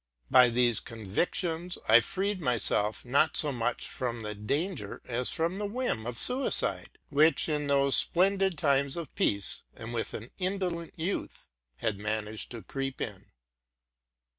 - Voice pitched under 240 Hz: Yes, medium, 140 Hz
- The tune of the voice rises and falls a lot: Yes, wide, 7.2 semitones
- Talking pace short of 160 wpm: Yes, average, 145 wpm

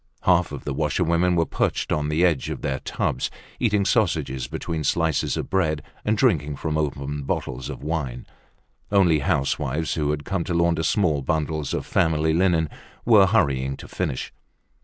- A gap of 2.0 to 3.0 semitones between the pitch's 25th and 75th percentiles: No, average, 3.6 semitones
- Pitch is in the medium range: No, very low, 80 Hz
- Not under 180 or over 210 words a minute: No, average, 165 wpm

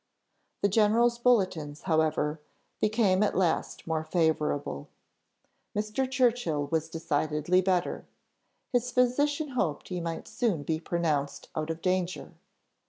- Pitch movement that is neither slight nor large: No, wide, 6.3 semitones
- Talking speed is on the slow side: Yes, slow, 115 wpm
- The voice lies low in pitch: No, medium, 180 Hz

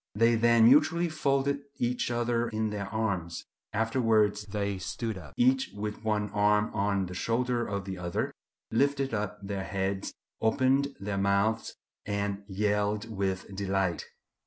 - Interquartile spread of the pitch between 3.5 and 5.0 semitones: No, average, 3.0 semitones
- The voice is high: No, low, 105 Hz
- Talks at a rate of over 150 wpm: No, average, 140 wpm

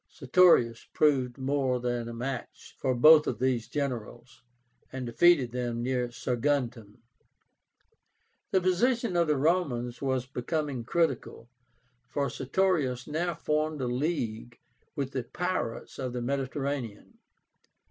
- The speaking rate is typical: No, slow, 120 wpm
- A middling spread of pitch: Yes, average, 3.9 semitones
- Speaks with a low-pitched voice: Yes, low, 130 Hz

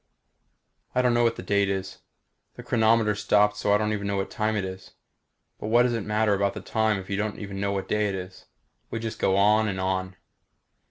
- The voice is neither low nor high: No, low, 105 Hz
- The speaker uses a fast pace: Yes, fast, 230 wpm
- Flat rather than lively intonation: Yes, narrow, 1.9 semitones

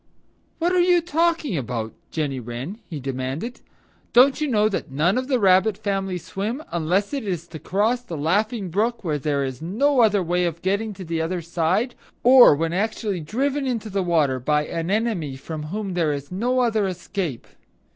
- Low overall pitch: No, high, 190 Hz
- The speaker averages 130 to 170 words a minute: No, average, 185 wpm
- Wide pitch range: Yes, wide, 6.2 semitones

